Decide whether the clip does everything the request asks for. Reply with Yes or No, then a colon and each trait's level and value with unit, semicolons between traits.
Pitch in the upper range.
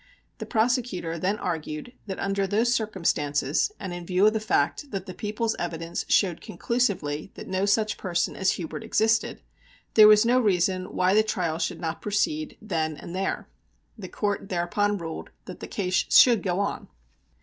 Yes: high, 195 Hz